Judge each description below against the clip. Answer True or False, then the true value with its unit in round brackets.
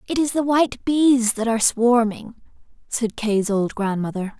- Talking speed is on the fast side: False (165 wpm)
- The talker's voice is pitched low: False (230 Hz)